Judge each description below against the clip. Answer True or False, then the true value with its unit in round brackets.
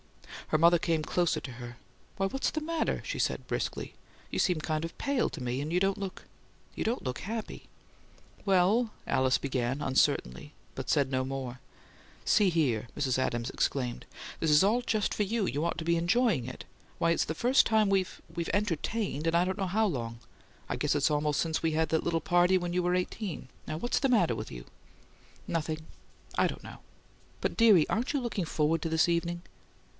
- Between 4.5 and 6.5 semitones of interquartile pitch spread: True (5.2 semitones)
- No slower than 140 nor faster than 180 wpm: False (200 wpm)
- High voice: False (170 Hz)